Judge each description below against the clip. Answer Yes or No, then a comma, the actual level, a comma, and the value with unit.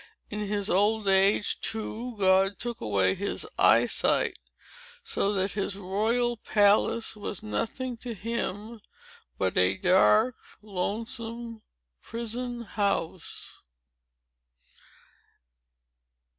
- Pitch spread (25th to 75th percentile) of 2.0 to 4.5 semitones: Yes, average, 3.2 semitones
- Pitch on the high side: Yes, high, 210 Hz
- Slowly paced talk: Yes, slow, 90 wpm